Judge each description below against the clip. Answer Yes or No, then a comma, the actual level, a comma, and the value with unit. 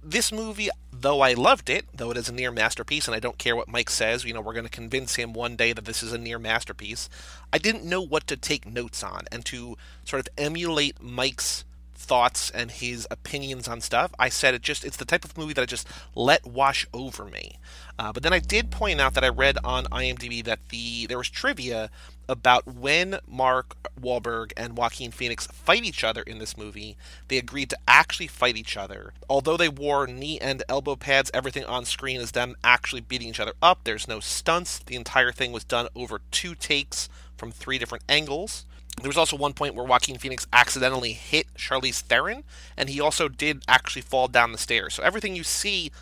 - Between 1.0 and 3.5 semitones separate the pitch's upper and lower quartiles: Yes, average, 3.2 semitones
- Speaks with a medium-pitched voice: No, low, 125 Hz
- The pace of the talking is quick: Yes, fast, 215 wpm